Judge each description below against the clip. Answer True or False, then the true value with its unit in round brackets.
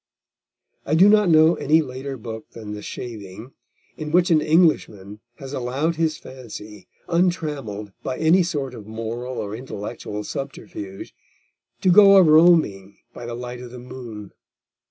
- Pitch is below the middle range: True (130 Hz)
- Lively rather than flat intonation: True (6.5 semitones)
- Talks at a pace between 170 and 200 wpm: False (150 wpm)